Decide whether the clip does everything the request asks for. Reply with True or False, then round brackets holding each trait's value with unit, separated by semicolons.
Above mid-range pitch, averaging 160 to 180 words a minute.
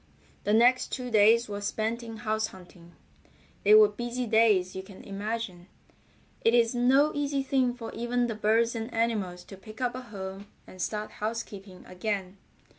True (220 Hz; 170 wpm)